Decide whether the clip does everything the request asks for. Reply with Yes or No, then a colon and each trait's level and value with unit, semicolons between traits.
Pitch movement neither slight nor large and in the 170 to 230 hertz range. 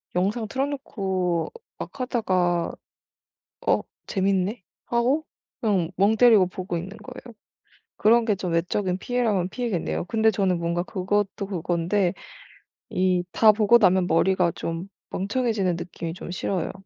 Yes: average, 3.7 semitones; high, 190 Hz